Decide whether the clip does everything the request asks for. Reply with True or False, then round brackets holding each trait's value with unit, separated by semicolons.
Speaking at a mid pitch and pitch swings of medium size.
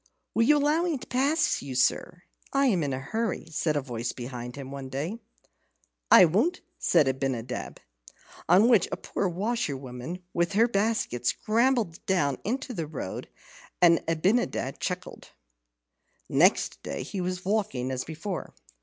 False (175 Hz; 8.9 semitones)